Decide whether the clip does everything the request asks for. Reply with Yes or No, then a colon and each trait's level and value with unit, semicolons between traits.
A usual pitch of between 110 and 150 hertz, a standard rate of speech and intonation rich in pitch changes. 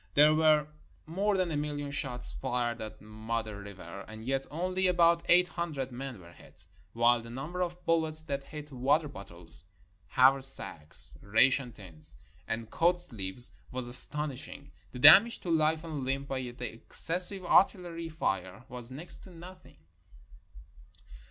Yes: low, 135 Hz; average, 150 wpm; wide, 6.0 semitones